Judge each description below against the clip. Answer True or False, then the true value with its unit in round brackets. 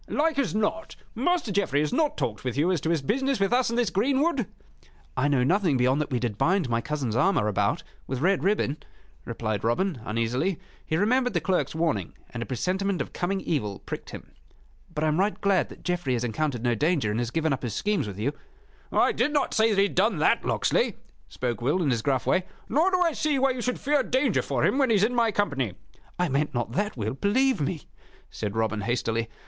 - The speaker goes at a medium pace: False (230 wpm)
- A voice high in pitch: False (170 Hz)